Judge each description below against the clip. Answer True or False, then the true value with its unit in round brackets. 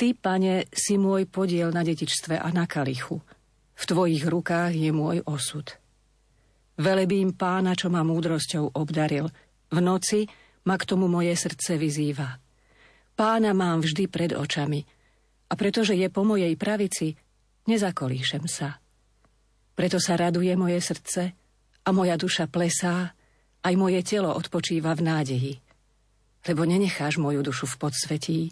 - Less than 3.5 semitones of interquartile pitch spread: False (3.8 semitones)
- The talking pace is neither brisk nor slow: True (135 wpm)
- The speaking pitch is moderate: True (170 Hz)